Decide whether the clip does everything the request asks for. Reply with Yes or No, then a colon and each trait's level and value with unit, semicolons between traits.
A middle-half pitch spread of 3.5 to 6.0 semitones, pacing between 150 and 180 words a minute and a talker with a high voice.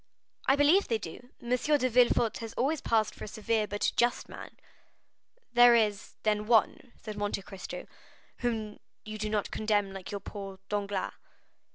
No: average, 2.7 semitones; average, 165 wpm; high, 220 Hz